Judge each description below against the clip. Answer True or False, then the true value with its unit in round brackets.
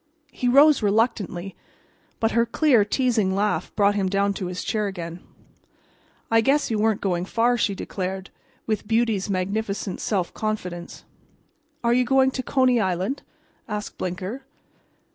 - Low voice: False (210 Hz)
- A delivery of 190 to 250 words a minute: False (145 wpm)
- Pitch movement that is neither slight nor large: True (3.7 semitones)